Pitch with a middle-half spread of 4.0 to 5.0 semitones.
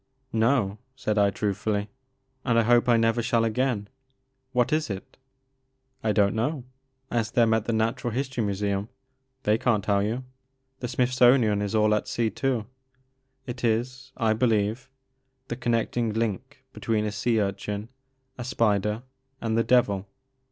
No: average, 2.8 semitones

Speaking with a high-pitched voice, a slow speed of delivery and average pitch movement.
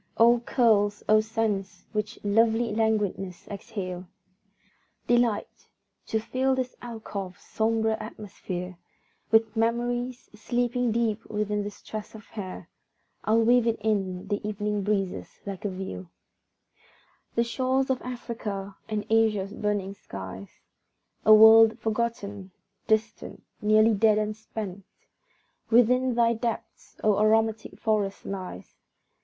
No: high, 215 Hz; slow, 115 wpm; narrow, 2.1 semitones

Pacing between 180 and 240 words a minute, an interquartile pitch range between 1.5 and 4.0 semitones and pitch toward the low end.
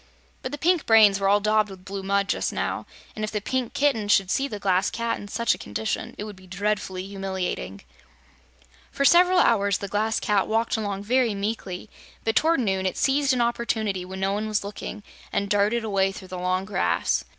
No: fast, 205 wpm; average, 2.7 semitones; high, 205 Hz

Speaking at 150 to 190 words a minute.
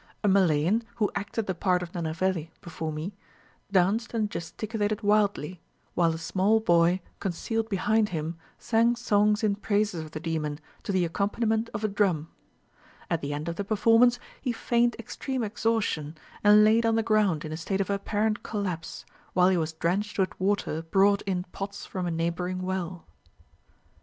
Yes: average, 170 wpm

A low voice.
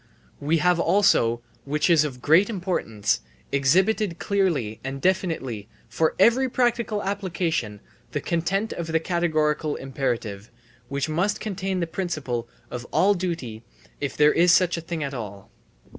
No: medium, 165 Hz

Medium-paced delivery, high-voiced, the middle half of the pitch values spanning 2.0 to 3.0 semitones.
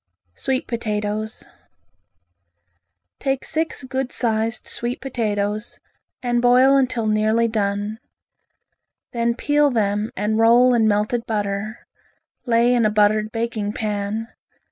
No: slow, 110 wpm; high, 225 Hz; narrow, 2.4 semitones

